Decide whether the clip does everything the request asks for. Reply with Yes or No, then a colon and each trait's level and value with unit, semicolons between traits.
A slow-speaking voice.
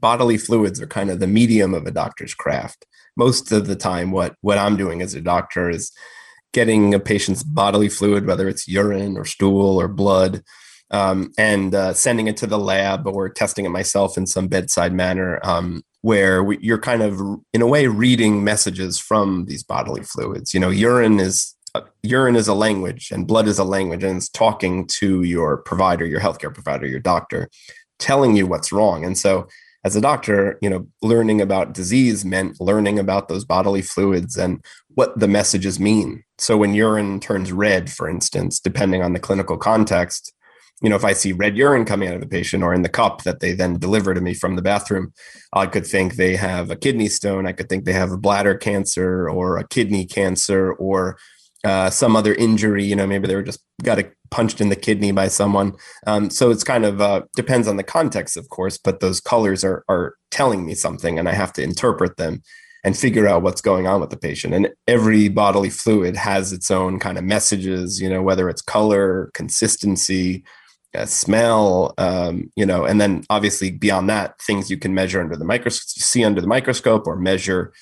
No: fast, 205 wpm